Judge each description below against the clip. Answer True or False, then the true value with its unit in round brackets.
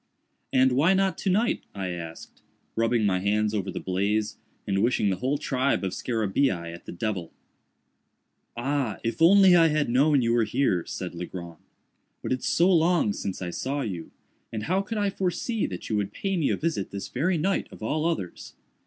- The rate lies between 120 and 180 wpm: False (190 wpm)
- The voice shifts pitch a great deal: True (8.9 semitones)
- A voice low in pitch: True (120 Hz)